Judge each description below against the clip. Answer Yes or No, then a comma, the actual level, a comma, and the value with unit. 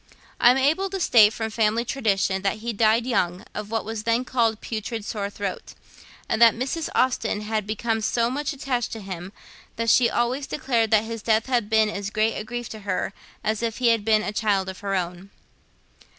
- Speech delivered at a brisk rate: Yes, fast, 210 wpm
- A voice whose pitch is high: Yes, high, 220 Hz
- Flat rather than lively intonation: Yes, narrow, 2.3 semitones